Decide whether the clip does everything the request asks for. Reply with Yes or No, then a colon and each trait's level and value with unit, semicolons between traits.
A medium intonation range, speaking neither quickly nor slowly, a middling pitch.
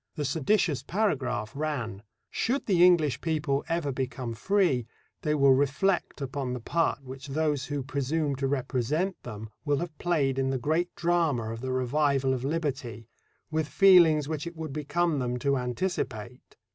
Yes: average, 3.9 semitones; average, 160 wpm; medium, 145 Hz